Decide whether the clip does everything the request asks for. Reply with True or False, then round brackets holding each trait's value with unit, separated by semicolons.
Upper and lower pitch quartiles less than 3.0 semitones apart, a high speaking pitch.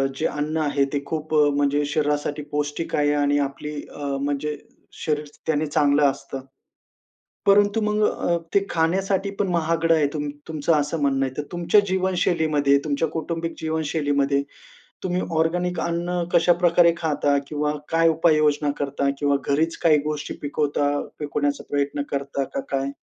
False (2.5 semitones; 150 Hz)